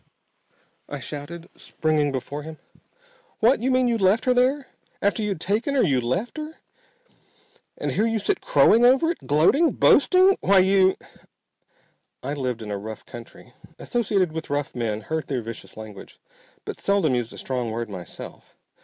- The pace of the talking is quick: No, average, 165 wpm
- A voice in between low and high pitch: Yes, medium, 160 Hz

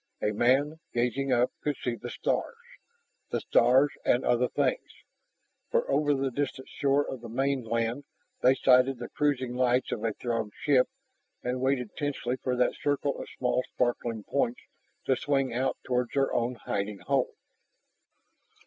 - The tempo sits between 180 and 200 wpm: No, average, 155 wpm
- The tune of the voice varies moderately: No, narrow, 2.3 semitones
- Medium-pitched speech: No, low, 125 Hz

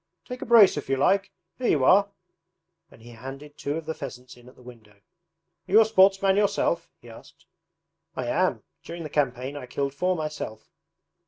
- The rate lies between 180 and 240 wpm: Yes, average, 190 wpm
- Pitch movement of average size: No, wide, 6.9 semitones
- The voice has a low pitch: No, medium, 150 Hz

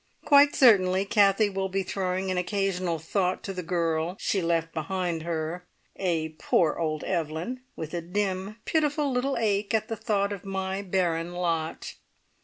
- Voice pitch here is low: No, medium, 185 Hz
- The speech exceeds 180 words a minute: No, average, 160 wpm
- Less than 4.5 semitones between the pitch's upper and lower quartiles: Yes, average, 3.1 semitones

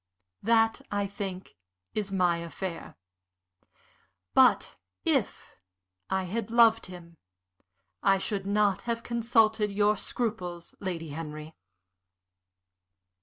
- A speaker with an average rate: No, slow, 95 wpm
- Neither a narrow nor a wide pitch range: Yes, average, 3.9 semitones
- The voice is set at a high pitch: Yes, high, 200 Hz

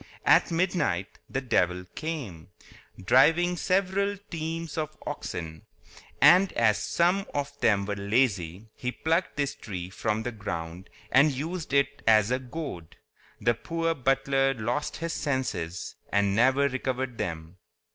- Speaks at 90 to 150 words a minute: Yes, slow, 135 wpm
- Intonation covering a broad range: Yes, wide, 7.7 semitones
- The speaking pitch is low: Yes, low, 130 Hz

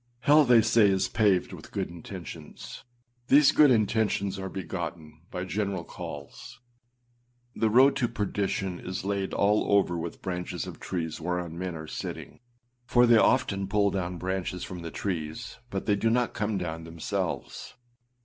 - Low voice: Yes, very low, 95 Hz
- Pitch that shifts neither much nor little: Yes, average, 3.9 semitones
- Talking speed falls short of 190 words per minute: Yes, average, 160 wpm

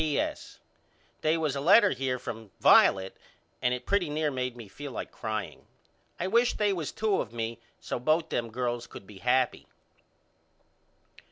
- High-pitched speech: No, low, 130 Hz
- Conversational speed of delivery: Yes, average, 165 wpm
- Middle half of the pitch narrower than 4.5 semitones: No, average, 5.1 semitones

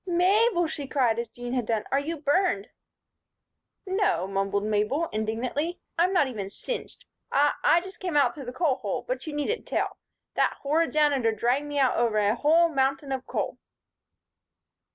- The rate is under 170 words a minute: No, average, 175 wpm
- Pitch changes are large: Yes, wide, 6.0 semitones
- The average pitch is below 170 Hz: No, very high, 280 Hz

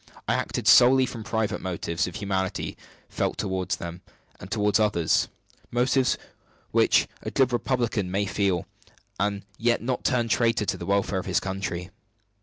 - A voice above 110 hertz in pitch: No, low, 100 Hz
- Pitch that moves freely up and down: No, average, 3.9 semitones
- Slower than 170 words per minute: Yes, average, 150 wpm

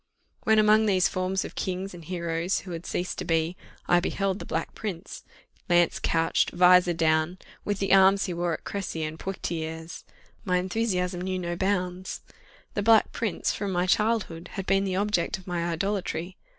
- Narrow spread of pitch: Yes, narrow, 2.3 semitones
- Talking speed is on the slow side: No, average, 175 wpm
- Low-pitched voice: No, medium, 180 Hz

